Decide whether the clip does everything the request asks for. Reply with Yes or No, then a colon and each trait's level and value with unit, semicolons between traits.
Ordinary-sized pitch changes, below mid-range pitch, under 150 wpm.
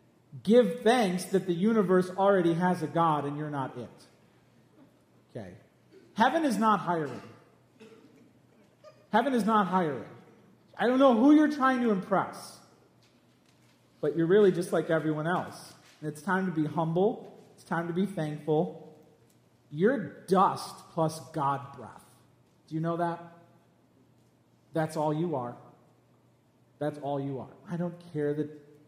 No: average, 4.4 semitones; medium, 170 Hz; average, 140 wpm